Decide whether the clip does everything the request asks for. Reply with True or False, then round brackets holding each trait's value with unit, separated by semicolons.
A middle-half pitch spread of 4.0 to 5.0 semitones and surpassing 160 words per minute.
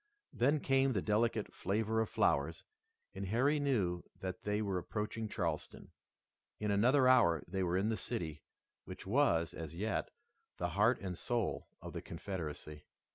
False (4.6 semitones; 155 wpm)